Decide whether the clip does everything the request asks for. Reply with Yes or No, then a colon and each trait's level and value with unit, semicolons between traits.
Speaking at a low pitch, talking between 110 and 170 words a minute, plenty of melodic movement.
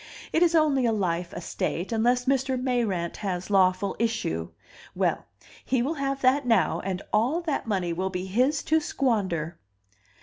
No: high, 225 Hz; average, 160 wpm; wide, 6.4 semitones